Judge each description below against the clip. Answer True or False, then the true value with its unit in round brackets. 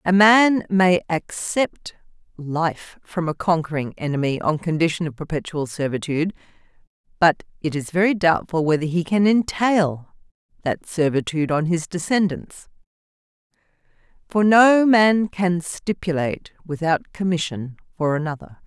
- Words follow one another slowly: True (120 wpm)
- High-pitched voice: False (170 Hz)